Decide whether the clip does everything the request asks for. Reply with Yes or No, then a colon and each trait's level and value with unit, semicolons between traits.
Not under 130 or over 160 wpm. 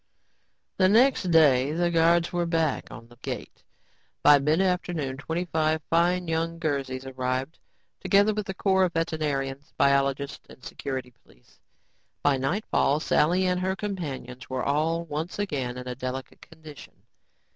Yes: average, 140 wpm